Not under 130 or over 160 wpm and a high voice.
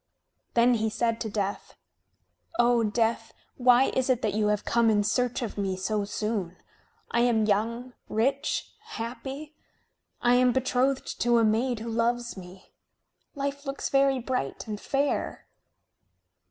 Yes: average, 145 wpm; high, 235 Hz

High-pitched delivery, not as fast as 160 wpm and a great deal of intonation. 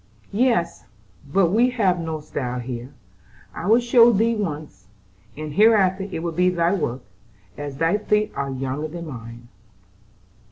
No: medium, 170 Hz; average, 150 wpm; wide, 7.0 semitones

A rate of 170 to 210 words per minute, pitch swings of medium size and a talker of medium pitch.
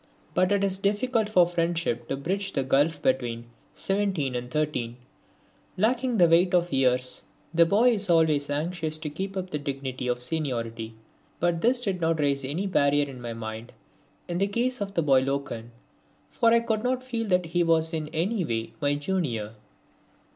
No: average, 180 wpm; wide, 6.2 semitones; medium, 165 Hz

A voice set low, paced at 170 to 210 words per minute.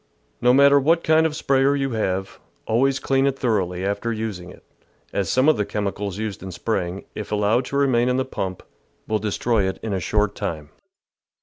Yes: low, 110 Hz; average, 200 wpm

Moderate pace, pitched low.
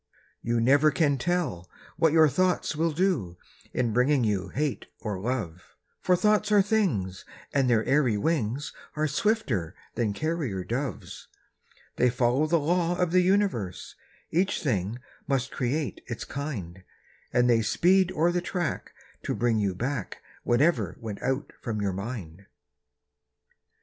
Yes: average, 145 wpm; low, 130 Hz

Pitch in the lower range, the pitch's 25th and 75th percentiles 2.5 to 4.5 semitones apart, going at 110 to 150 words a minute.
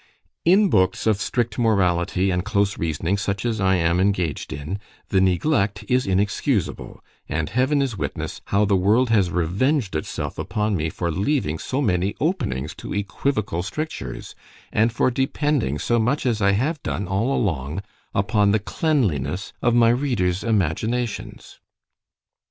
No: low, 100 Hz; average, 5.0 semitones; average, 145 wpm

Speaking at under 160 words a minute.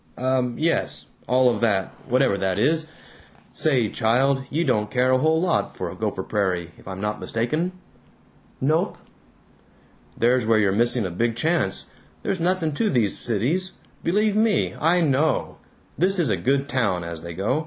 No: average, 165 wpm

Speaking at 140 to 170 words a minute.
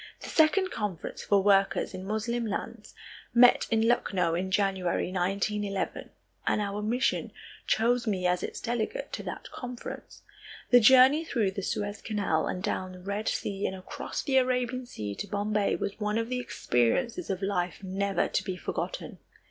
Yes: average, 165 wpm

